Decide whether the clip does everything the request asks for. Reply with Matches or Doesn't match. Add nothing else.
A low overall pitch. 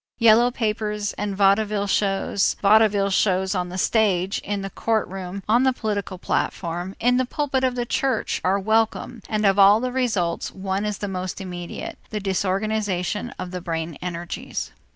Doesn't match